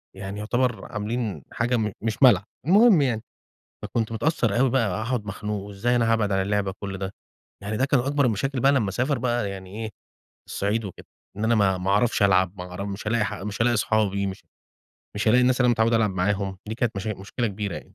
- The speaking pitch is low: Yes, low, 110 Hz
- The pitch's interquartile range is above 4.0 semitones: No, average, 3.4 semitones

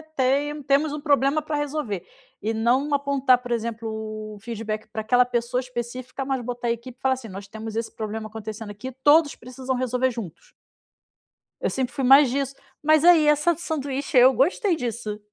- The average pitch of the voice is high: Yes, very high, 255 Hz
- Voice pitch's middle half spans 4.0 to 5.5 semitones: No, average, 3.6 semitones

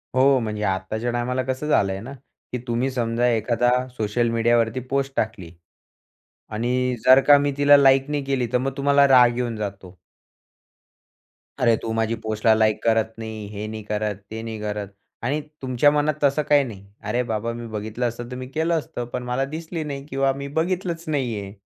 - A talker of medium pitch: No, low, 120 Hz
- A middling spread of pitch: Yes, average, 3.6 semitones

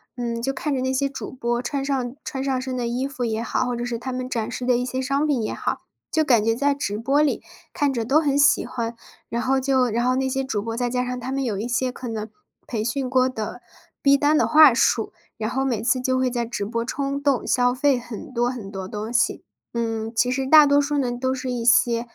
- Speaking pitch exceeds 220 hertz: Yes, very high, 250 Hz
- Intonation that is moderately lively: No, narrow, 2.3 semitones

